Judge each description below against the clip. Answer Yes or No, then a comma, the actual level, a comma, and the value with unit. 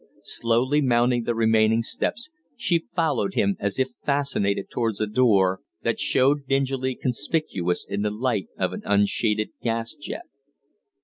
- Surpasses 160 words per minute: No, average, 140 wpm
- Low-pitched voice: Yes, low, 120 Hz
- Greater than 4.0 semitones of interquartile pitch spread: Yes, average, 4.4 semitones